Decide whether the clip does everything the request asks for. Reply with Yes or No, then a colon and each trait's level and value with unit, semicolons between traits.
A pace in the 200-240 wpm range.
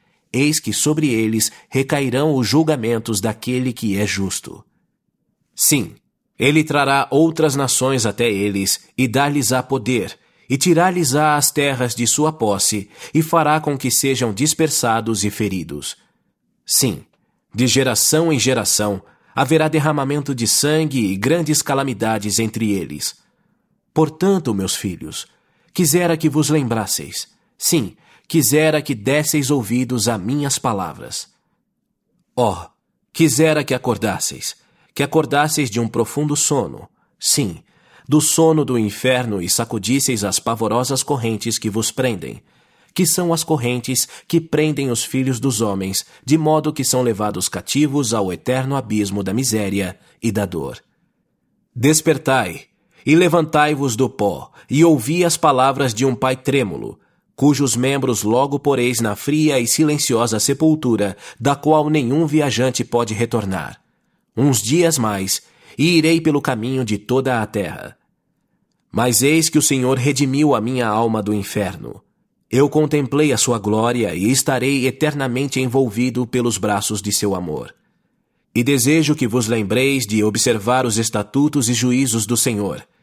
No: average, 140 wpm